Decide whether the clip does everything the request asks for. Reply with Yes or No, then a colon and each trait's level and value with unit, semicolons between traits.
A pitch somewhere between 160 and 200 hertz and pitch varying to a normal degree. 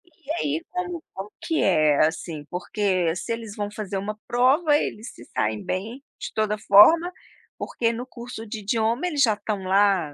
No: high, 210 Hz; average, 4.8 semitones